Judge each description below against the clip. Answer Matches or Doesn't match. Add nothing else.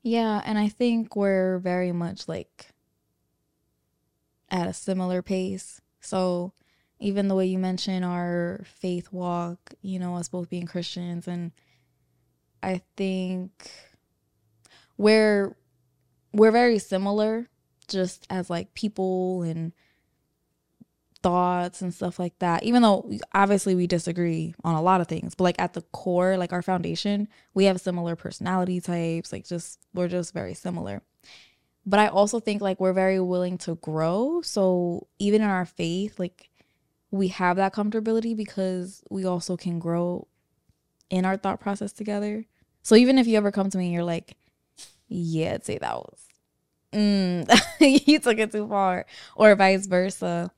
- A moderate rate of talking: Matches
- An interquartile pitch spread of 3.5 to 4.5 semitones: Doesn't match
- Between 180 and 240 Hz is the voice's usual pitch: Matches